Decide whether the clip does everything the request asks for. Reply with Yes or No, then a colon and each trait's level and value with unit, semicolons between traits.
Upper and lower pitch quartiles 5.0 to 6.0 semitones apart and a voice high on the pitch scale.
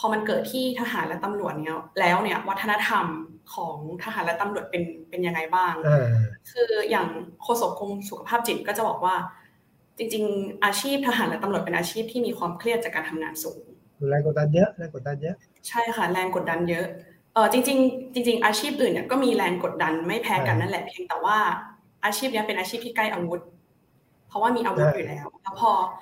Yes: wide, 5.4 semitones; high, 200 Hz